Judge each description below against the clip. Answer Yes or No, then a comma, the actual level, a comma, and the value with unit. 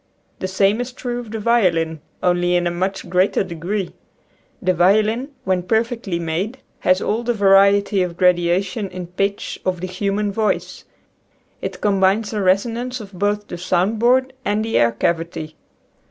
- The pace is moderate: Yes, average, 160 wpm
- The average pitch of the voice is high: Yes, high, 195 Hz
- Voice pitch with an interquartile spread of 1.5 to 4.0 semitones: Yes, average, 3.3 semitones